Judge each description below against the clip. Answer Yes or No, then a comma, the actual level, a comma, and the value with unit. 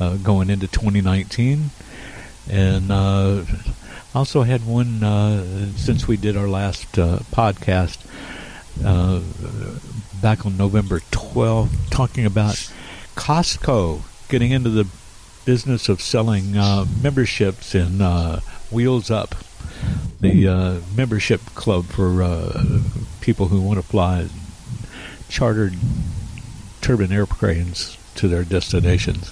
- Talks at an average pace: No, slow, 110 wpm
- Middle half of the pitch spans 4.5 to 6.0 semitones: No, average, 3.8 semitones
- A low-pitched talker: Yes, low, 100 Hz